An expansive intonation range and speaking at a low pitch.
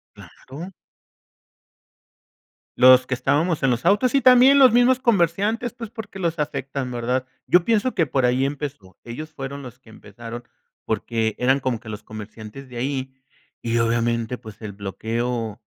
Yes: wide, 6.8 semitones; low, 130 Hz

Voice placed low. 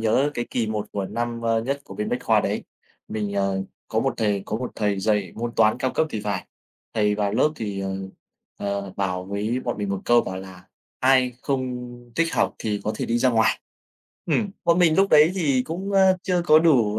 Yes: low, 110 Hz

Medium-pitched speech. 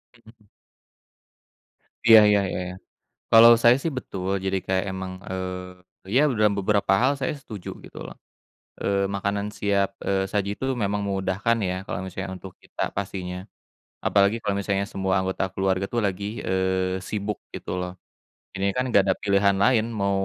No: low, 100 Hz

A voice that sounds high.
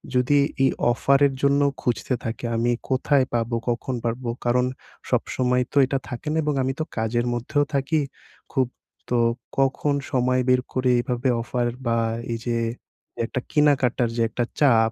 No: low, 125 Hz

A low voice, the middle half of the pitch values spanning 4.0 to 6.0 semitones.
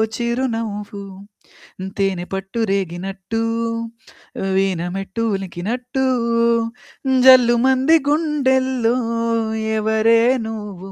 No: high, 220 Hz; average, 4.5 semitones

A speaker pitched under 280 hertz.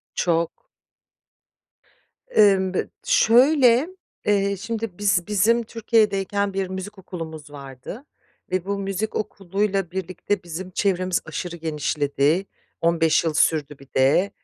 Yes: high, 190 Hz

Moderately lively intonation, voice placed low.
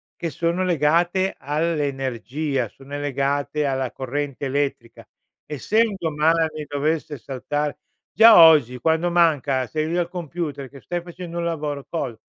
No: average, 3.4 semitones; medium, 150 Hz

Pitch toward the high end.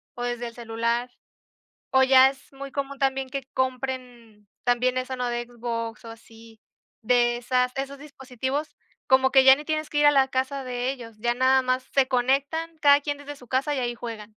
Yes: very high, 260 Hz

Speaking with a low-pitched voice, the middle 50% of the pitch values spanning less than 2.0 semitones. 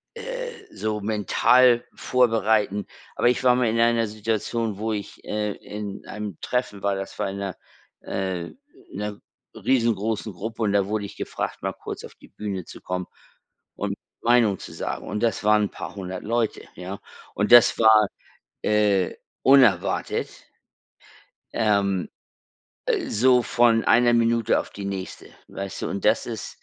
No: low, 105 Hz; average, 2.7 semitones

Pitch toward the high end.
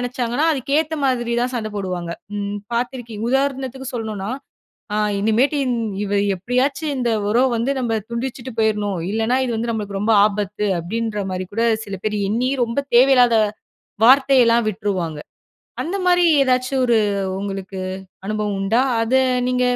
Yes: high, 230 Hz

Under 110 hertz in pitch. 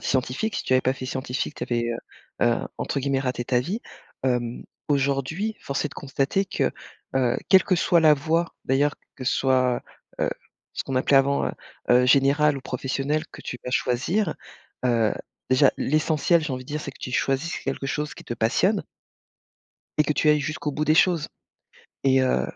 No: low, 135 Hz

